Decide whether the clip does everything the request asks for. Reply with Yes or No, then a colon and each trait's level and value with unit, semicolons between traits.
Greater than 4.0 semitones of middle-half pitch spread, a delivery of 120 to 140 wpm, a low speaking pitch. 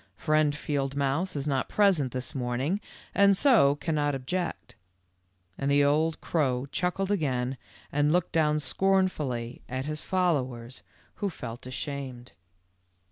No: average, 4.5 semitones; slow, 135 wpm; medium, 145 Hz